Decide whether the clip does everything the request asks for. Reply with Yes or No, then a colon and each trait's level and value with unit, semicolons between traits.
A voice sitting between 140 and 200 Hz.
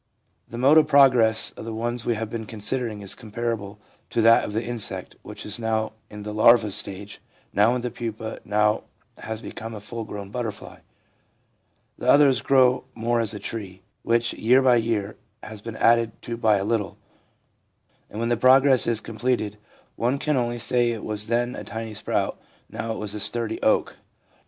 No: low, 115 Hz